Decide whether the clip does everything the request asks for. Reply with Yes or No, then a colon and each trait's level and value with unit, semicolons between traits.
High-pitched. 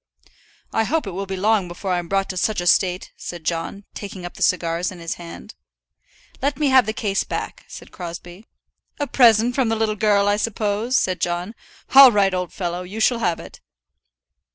Yes: high, 195 Hz